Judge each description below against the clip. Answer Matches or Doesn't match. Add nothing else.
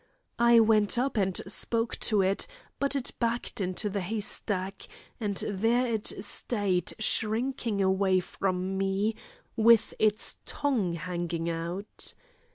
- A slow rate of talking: Matches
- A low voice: Doesn't match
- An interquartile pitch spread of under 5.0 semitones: Matches